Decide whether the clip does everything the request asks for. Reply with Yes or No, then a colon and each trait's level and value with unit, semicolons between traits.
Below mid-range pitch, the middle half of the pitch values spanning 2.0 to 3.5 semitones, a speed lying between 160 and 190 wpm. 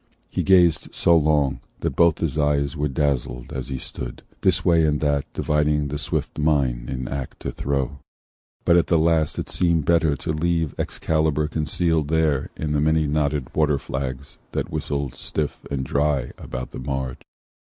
Yes: very low, 75 Hz; narrow, 2.4 semitones; average, 170 wpm